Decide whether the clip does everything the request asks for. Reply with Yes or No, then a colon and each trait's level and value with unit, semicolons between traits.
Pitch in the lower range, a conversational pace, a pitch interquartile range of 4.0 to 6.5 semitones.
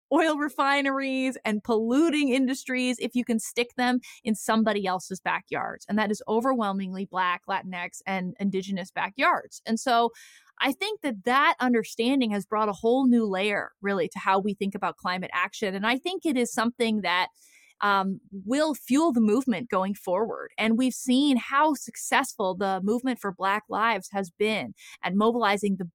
No: high, 220 Hz; average, 170 wpm; average, 4.4 semitones